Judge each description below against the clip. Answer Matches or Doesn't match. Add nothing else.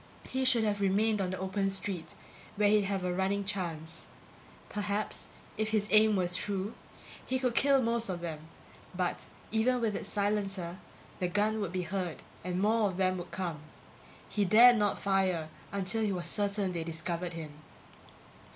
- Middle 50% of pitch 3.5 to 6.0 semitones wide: Doesn't match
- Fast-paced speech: Doesn't match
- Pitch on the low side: Doesn't match